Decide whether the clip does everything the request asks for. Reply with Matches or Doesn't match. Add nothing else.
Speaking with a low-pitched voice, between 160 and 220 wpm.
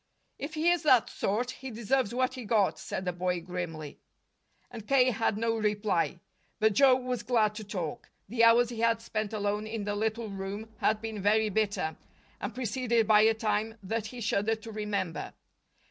Doesn't match